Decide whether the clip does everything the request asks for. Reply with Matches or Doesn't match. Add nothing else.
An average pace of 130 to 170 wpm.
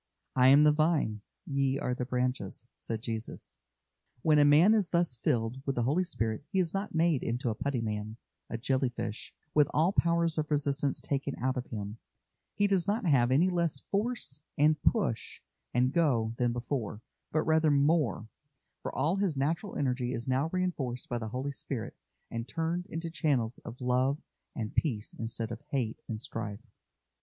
Doesn't match